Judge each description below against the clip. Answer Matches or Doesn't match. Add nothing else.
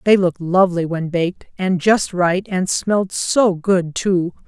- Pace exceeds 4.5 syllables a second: Doesn't match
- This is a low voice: Doesn't match